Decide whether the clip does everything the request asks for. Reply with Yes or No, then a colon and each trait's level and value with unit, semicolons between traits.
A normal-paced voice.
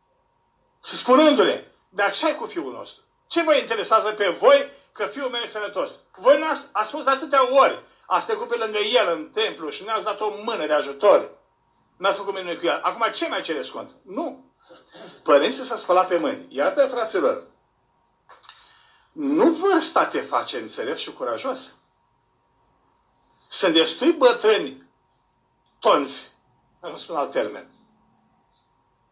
Yes: average, 155 wpm